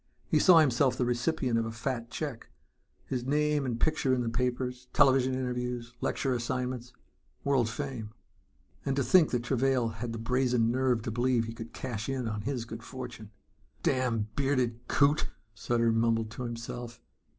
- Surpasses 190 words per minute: No, average, 165 wpm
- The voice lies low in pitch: Yes, low, 125 Hz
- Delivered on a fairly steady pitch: Yes, narrow, 2.2 semitones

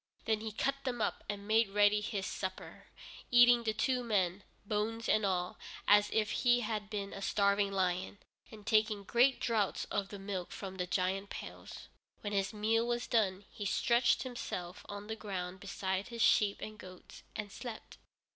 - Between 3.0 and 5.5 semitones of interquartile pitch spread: No, narrow, 2.4 semitones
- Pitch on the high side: Yes, high, 210 Hz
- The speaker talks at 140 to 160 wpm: No, average, 175 wpm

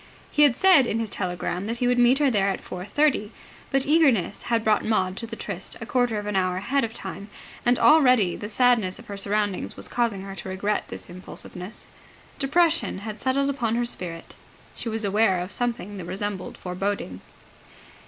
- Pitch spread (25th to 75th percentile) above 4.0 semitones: Yes, average, 4.4 semitones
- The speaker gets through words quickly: No, average, 195 wpm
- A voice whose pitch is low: No, high, 215 Hz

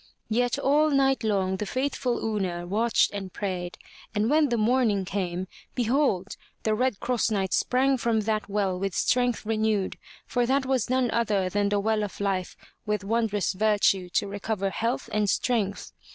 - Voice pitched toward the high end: Yes, high, 215 Hz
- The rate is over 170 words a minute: No, average, 165 wpm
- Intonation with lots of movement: No, average, 3.7 semitones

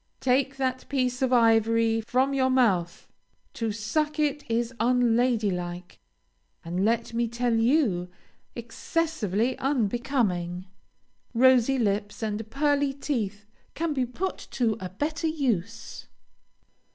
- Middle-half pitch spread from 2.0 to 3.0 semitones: No, average, 3.9 semitones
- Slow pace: Yes, slow, 115 wpm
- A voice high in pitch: Yes, high, 240 Hz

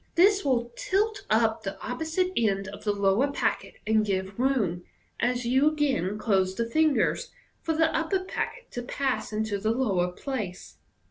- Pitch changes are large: Yes, wide, 7.0 semitones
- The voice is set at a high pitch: Yes, high, 240 Hz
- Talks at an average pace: Yes, average, 160 wpm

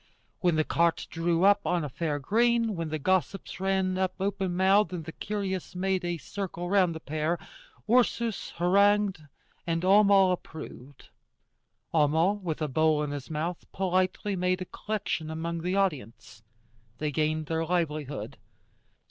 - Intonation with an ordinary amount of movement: Yes, average, 3.5 semitones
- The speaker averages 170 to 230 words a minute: No, average, 150 wpm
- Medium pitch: Yes, medium, 175 Hz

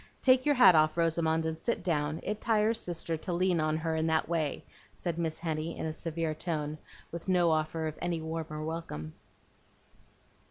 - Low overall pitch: No, medium, 165 Hz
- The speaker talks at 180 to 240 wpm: Yes, average, 185 wpm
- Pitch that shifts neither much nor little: No, narrow, 1.8 semitones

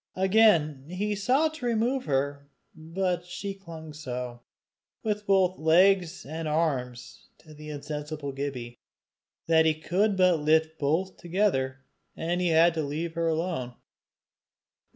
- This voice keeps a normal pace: No, slow, 130 wpm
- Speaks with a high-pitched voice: No, medium, 160 Hz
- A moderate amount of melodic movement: Yes, average, 4.2 semitones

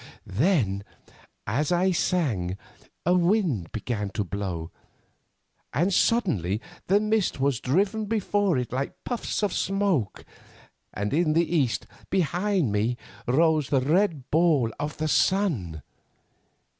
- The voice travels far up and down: Yes, wide, 8.8 semitones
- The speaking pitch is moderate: Yes, medium, 155 Hz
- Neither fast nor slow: No, slow, 120 wpm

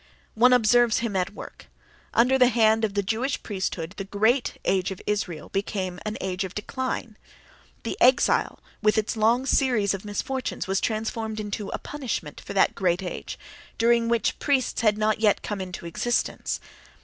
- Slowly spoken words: No, average, 165 wpm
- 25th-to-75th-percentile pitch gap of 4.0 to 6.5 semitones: No, average, 3.4 semitones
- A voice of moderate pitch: No, high, 215 Hz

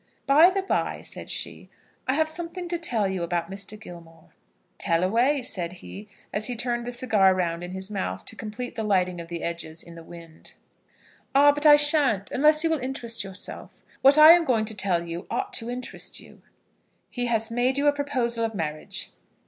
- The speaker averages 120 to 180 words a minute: No, average, 200 wpm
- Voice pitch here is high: Yes, high, 225 Hz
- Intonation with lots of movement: Yes, wide, 7.6 semitones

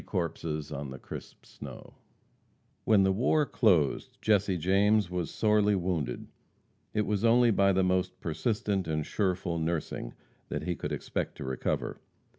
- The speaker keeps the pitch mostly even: No, average, 4.2 semitones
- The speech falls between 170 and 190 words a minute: No, average, 145 wpm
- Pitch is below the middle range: Yes, very low, 95 Hz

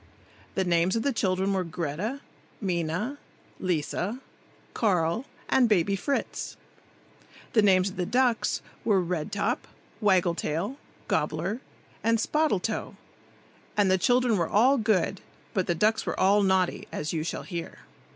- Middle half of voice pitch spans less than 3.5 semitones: No, average, 4.2 semitones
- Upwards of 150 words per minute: No, average, 140 wpm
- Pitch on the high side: Yes, high, 195 Hz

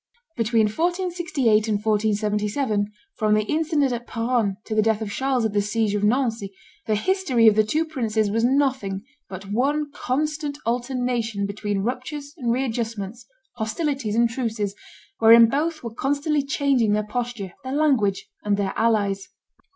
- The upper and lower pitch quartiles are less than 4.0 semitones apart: No, average, 4.4 semitones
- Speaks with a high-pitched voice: Yes, high, 230 Hz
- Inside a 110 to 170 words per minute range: Yes, average, 155 wpm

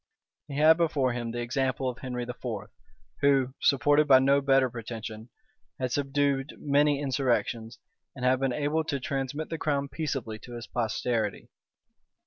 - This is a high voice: No, low, 135 Hz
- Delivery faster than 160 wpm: No, average, 150 wpm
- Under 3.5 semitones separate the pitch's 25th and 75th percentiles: Yes, average, 2.8 semitones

